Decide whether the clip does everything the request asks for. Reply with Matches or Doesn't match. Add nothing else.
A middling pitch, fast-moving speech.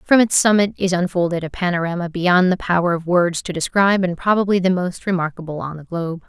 Matches